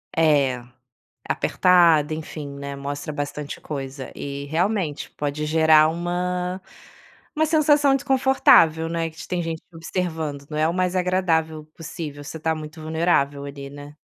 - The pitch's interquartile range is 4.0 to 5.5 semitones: No, average, 3.4 semitones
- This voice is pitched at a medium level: Yes, medium, 160 Hz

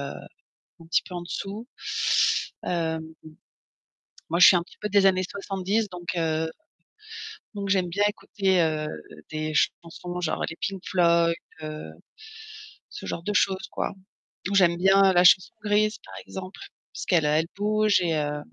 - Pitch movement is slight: No, average, 3.1 semitones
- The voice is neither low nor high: Yes, medium, 180 Hz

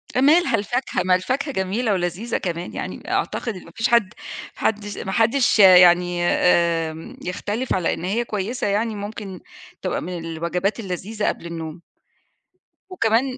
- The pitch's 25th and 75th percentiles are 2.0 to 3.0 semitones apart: No, average, 4.3 semitones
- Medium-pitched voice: No, high, 200 Hz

